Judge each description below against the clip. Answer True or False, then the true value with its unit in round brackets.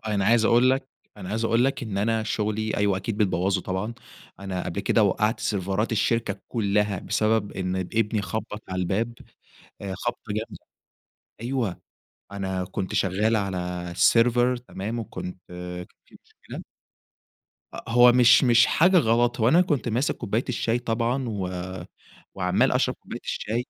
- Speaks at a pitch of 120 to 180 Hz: False (110 Hz)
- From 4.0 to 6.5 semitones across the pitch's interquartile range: False (3.3 semitones)